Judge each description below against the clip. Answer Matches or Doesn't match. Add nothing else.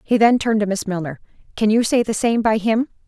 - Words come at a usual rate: Doesn't match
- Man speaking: Doesn't match